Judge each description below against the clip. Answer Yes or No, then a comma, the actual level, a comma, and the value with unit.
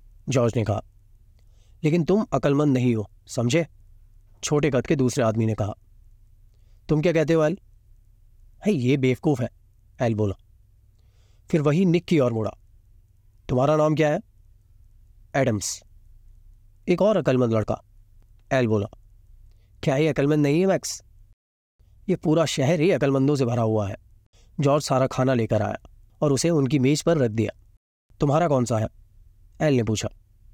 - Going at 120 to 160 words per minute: Yes, average, 145 wpm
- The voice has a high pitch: No, low, 110 Hz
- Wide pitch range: Yes, wide, 5.8 semitones